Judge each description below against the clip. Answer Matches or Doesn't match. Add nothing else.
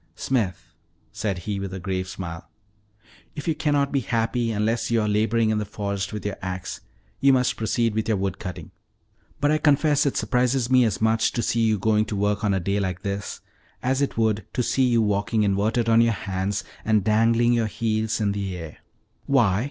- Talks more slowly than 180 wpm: Doesn't match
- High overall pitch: Doesn't match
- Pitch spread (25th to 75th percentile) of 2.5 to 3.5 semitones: Matches